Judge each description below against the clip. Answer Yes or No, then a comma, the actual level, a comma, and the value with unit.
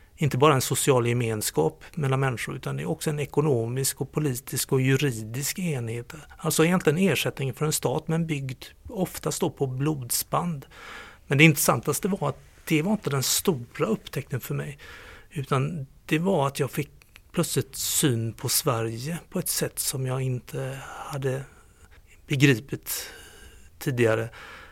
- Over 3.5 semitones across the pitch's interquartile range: No, average, 3.0 semitones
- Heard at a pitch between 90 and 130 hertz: No, medium, 140 Hz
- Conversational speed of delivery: Yes, average, 150 wpm